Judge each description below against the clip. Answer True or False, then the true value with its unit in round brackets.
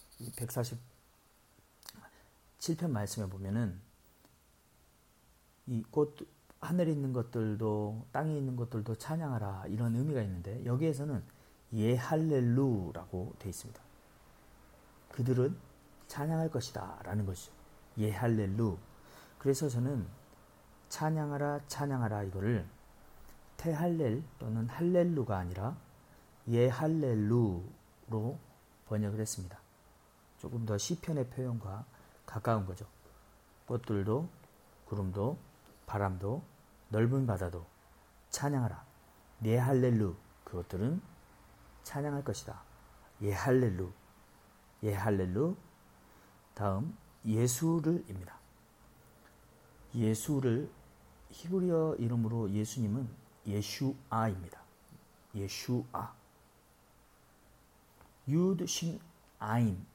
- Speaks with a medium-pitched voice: False (115 Hz)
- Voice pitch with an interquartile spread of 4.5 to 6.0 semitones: True (5.4 semitones)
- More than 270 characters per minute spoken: False (200 characters per minute)